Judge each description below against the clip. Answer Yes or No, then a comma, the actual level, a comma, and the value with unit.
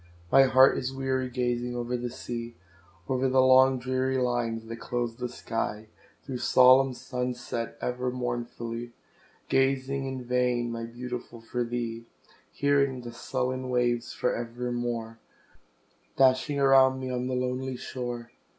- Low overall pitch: Yes, low, 125 Hz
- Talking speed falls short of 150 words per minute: Yes, average, 140 wpm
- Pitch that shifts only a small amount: Yes, narrow, 1.4 semitones